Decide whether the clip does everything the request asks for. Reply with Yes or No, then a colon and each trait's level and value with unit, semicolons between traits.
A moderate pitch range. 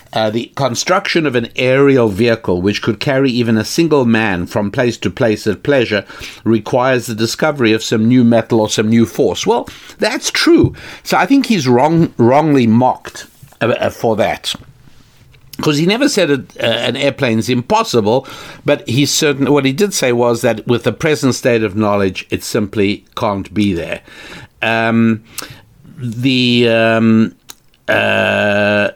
Yes: average, 3.7 semitones